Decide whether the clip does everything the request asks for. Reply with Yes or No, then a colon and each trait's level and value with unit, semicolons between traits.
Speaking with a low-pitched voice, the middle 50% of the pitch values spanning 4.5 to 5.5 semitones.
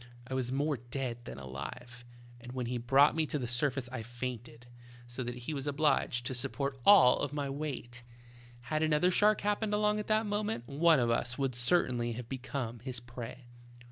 No: low, 130 Hz; average, 3.8 semitones